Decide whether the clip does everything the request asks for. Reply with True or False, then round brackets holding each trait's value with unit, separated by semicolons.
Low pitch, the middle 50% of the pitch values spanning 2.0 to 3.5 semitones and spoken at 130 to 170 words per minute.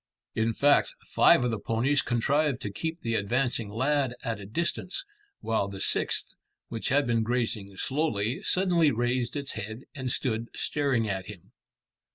False (120 Hz; 4.2 semitones; 160 wpm)